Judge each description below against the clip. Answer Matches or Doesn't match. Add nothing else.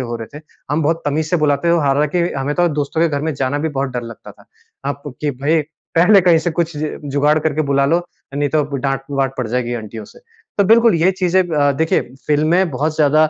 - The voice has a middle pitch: Matches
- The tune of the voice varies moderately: Matches